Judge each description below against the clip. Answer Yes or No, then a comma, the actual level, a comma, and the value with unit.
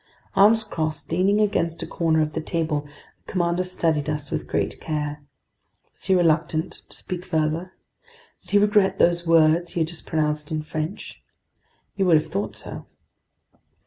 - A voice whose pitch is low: No, medium, 165 Hz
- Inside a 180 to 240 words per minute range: No, average, 165 wpm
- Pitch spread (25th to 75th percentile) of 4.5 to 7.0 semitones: No, average, 2.8 semitones